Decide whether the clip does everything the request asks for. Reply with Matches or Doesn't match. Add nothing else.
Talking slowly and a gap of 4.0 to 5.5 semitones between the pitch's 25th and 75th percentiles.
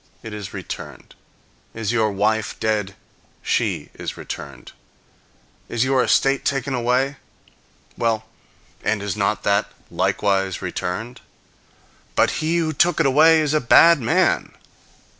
Matches